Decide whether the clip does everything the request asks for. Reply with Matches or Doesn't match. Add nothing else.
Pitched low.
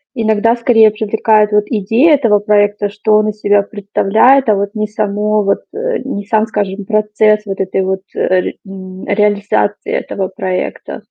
Doesn't match